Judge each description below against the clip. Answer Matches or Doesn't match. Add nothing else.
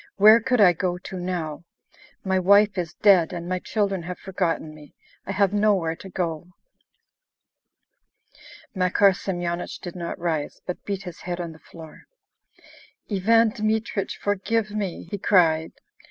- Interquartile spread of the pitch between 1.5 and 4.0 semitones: Matches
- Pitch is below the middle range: Doesn't match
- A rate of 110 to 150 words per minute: Matches